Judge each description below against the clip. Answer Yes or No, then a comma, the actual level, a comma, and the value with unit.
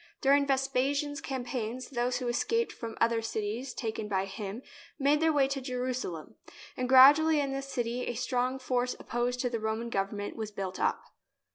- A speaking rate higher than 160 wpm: Yes, average, 175 wpm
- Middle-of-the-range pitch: No, very high, 250 Hz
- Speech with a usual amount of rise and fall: Yes, average, 3.1 semitones